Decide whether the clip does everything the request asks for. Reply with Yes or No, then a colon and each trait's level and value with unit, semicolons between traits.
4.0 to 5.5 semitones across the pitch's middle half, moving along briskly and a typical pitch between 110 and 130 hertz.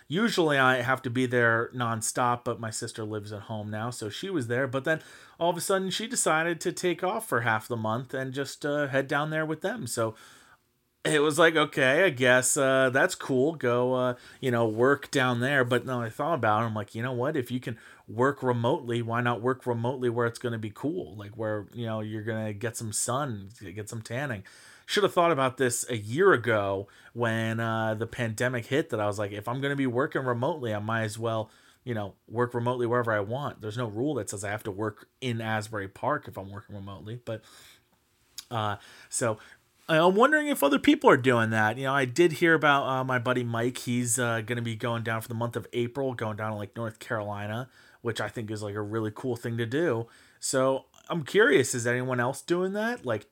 No: average, 3.1 semitones; fast, 235 wpm; low, 120 Hz